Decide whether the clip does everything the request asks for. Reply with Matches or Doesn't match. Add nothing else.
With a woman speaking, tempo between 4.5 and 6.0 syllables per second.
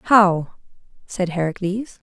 Doesn't match